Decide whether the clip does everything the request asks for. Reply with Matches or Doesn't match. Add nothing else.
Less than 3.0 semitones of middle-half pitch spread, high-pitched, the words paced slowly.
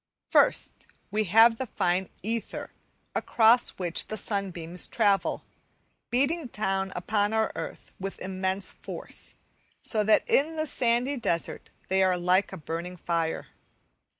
Doesn't match